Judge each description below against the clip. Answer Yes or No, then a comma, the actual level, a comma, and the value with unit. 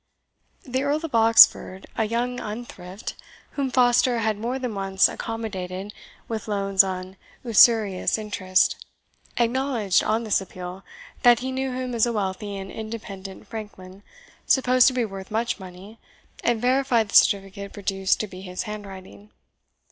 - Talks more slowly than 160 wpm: Yes, average, 145 wpm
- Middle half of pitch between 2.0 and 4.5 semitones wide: Yes, average, 3.8 semitones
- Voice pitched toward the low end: No, high, 215 Hz